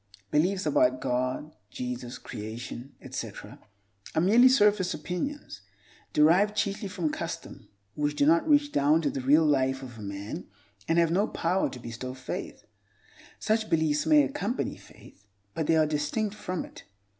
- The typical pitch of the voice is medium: Yes, medium, 160 Hz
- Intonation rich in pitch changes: Yes, wide, 7.6 semitones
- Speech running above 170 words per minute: No, average, 155 wpm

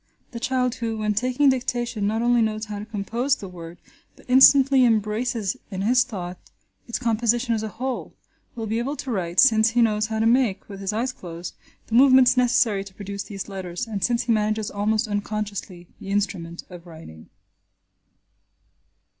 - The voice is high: Yes, high, 220 Hz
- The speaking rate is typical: Yes, average, 180 wpm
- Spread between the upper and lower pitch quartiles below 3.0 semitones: No, average, 3.5 semitones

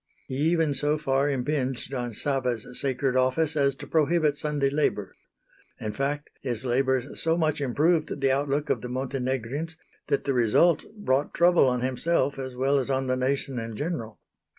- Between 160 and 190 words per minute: Yes, average, 170 wpm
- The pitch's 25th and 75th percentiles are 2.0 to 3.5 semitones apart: Yes, narrow, 2.6 semitones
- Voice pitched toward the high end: No, low, 135 Hz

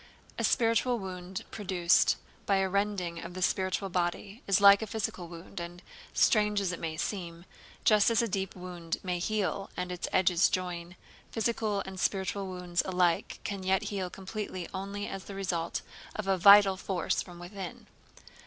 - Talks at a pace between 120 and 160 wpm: No, average, 170 wpm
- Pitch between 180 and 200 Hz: Yes, high, 190 Hz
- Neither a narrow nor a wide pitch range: No, narrow, 2.1 semitones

